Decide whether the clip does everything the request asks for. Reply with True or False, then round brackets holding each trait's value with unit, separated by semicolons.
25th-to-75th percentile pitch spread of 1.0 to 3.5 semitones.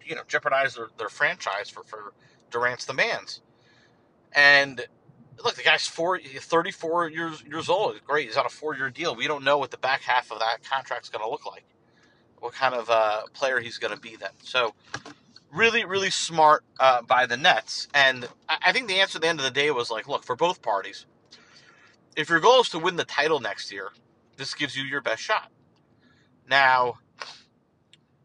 False (4.8 semitones)